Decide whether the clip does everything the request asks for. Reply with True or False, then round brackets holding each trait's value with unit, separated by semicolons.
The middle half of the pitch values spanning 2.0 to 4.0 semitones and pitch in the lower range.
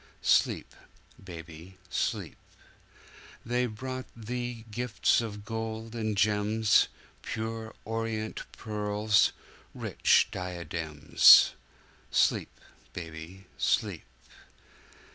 True (3.2 semitones; 110 Hz)